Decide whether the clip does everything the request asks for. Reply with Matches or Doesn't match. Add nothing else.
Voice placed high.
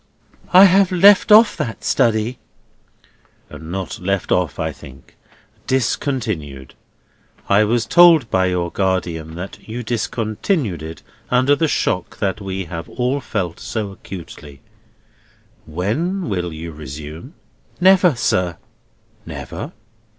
Doesn't match